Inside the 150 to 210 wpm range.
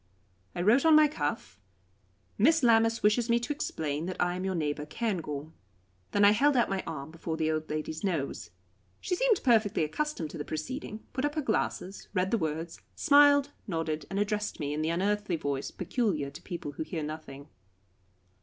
Yes: average, 185 wpm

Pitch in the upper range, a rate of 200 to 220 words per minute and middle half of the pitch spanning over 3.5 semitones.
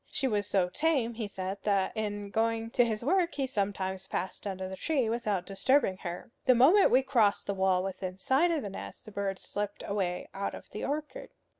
Yes: high, 205 Hz; fast, 205 wpm; average, 4.9 semitones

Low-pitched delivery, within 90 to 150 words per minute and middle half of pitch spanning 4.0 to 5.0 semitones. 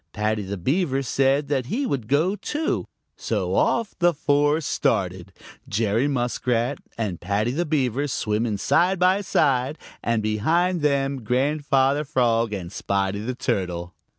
No: low, 130 Hz; average, 140 wpm; wide, 5.5 semitones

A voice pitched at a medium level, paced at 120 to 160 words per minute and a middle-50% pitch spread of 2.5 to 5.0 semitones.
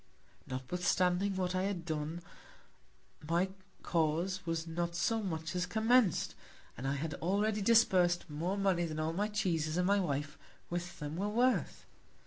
Yes: medium, 175 Hz; average, 150 wpm; average, 3.5 semitones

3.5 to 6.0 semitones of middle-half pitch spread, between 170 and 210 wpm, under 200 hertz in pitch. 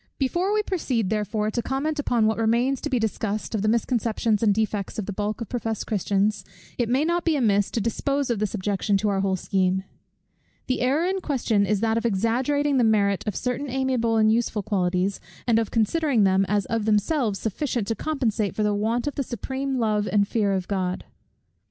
No: average, 4.0 semitones; fast, 205 wpm; high, 220 Hz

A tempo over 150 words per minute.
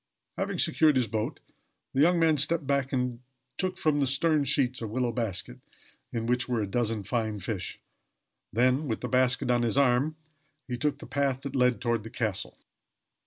Yes: average, 190 wpm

